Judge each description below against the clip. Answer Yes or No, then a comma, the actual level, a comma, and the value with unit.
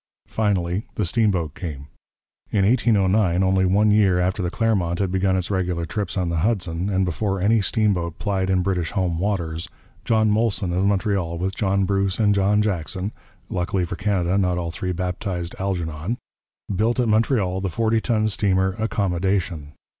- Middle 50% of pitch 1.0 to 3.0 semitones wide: Yes, average, 2.7 semitones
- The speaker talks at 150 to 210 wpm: Yes, average, 165 wpm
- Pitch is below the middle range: Yes, very low, 95 Hz